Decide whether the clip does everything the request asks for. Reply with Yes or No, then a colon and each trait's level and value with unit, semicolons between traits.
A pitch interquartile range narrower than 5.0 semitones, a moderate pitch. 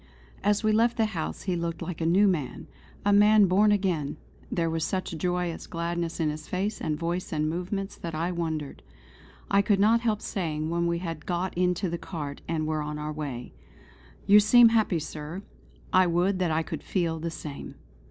Yes: average, 3.6 semitones; medium, 175 Hz